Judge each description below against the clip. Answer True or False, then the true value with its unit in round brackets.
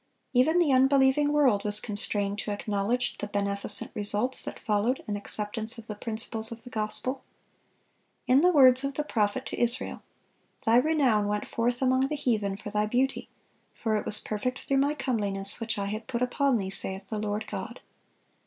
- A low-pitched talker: False (225 Hz)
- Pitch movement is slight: False (4.0 semitones)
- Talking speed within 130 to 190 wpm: True (180 wpm)